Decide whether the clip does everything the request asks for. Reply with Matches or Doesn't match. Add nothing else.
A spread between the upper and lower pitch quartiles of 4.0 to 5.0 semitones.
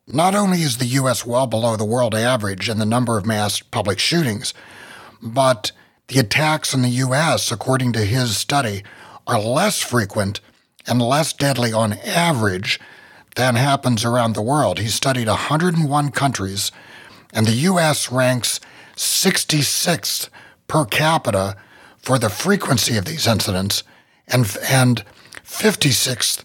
Matches